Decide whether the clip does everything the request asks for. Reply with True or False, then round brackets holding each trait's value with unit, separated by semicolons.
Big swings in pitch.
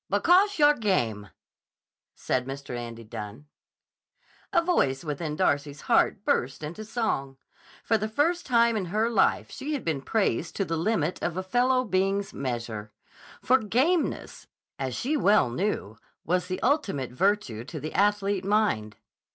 True (8.9 semitones)